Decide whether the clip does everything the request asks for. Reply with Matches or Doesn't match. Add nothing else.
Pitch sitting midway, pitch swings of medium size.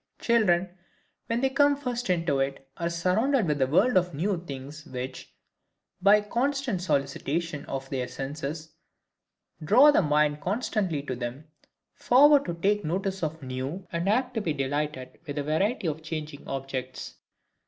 Doesn't match